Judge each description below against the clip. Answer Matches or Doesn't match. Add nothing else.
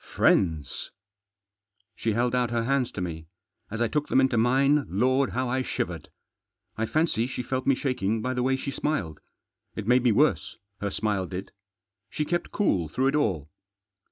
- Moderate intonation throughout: Matches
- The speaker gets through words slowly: Doesn't match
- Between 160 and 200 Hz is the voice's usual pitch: Doesn't match